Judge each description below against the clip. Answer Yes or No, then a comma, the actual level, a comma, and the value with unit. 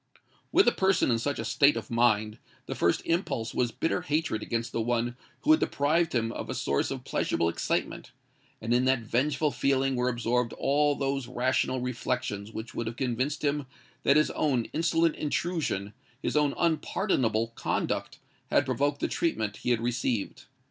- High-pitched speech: No, low, 125 Hz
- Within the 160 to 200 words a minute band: Yes, average, 170 wpm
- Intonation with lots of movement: No, average, 4.1 semitones